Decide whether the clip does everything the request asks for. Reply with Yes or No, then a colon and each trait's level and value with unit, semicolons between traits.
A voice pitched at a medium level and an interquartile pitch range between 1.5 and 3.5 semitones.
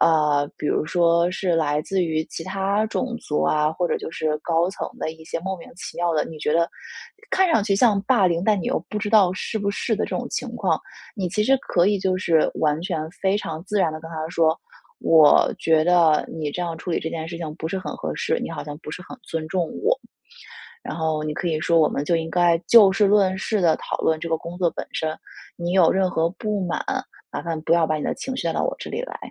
Yes: medium, 170 Hz; average, 3.2 semitones